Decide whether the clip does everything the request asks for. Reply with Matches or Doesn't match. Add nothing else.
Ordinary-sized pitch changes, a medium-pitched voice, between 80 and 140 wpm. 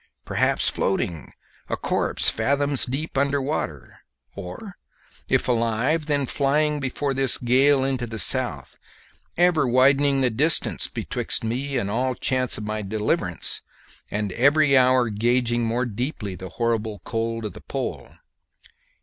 Doesn't match